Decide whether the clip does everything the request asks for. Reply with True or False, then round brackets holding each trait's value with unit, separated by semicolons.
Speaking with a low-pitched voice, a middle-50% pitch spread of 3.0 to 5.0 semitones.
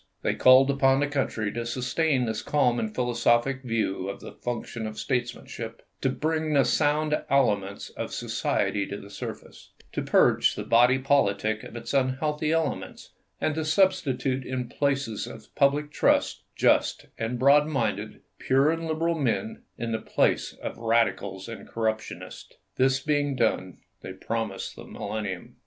True (130 Hz; 4.2 semitones)